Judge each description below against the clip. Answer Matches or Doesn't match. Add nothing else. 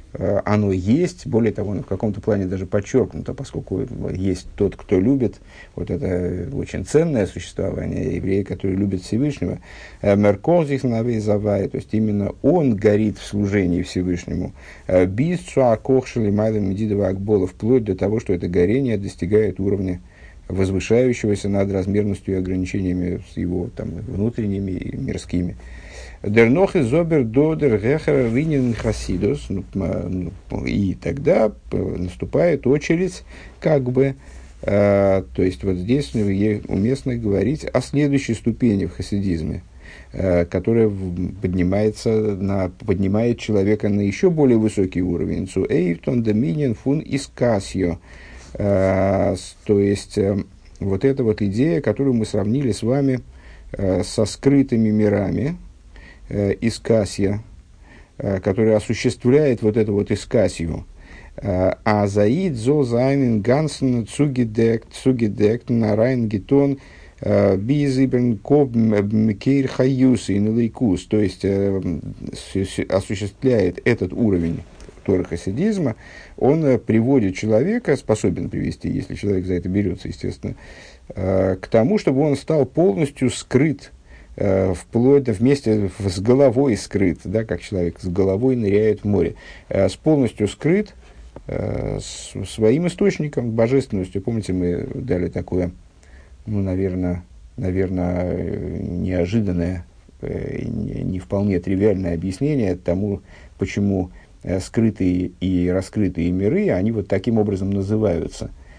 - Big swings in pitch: Doesn't match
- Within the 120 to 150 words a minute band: Doesn't match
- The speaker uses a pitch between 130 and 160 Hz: Doesn't match